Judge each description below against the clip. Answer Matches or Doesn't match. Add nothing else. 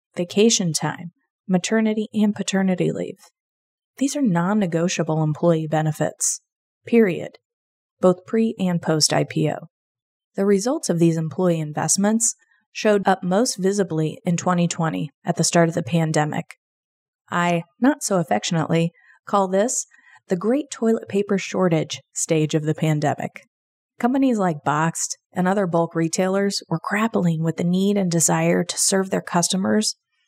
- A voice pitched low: Doesn't match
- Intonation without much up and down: Doesn't match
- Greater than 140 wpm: Doesn't match